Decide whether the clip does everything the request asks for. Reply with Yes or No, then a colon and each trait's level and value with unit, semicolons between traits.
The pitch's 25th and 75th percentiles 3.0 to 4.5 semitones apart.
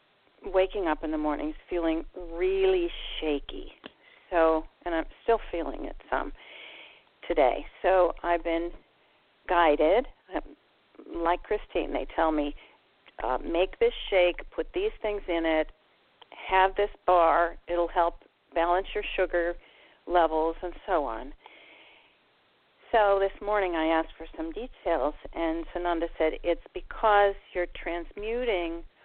Yes: average, 3.7 semitones